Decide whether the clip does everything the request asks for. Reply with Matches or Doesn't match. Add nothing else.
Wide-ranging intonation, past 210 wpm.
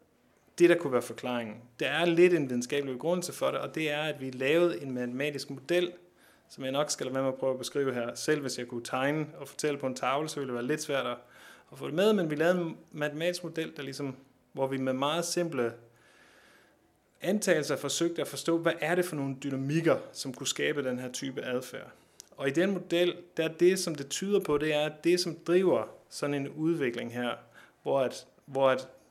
Doesn't match